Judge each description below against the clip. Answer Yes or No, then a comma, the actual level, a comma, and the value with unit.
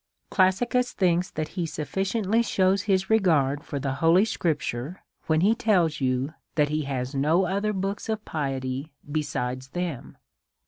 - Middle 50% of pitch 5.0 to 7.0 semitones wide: Yes, wide, 5.6 semitones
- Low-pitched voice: No, medium, 165 Hz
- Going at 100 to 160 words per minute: Yes, average, 145 wpm